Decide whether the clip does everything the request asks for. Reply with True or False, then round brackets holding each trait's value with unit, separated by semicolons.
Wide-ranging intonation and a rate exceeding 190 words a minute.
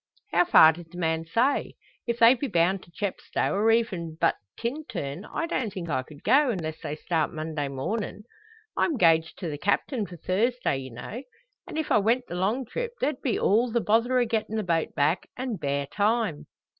True (6.6 semitones; 200 wpm)